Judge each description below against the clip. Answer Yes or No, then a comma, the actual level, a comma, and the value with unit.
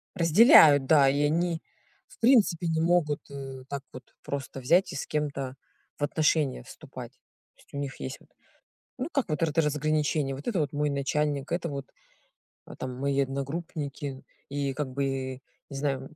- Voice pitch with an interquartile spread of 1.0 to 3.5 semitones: Yes, average, 2.7 semitones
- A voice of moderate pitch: Yes, medium, 145 Hz